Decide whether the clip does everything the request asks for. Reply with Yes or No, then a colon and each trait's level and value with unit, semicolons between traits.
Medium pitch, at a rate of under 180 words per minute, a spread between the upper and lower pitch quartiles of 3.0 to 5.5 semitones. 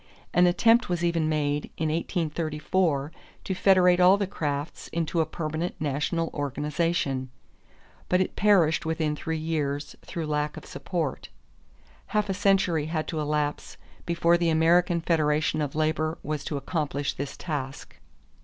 No: medium, 160 Hz; average, 145 wpm; narrow, 2.6 semitones